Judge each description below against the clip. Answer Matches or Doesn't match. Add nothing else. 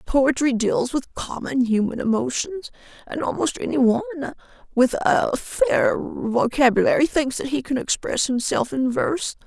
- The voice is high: Matches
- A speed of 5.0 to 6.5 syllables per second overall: Doesn't match